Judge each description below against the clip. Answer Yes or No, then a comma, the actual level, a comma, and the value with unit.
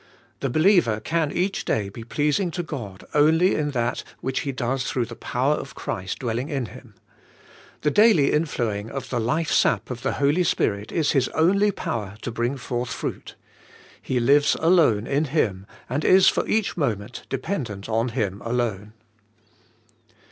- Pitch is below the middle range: Yes, low, 130 Hz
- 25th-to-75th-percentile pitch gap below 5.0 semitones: No, average, 5.3 semitones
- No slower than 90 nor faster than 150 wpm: No, average, 165 wpm